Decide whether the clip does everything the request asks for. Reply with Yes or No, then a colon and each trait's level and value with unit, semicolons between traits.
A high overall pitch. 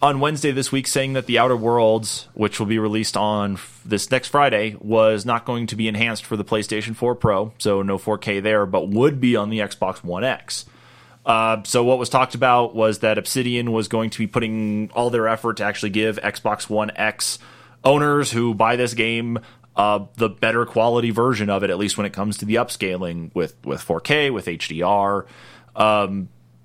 No: low, 110 Hz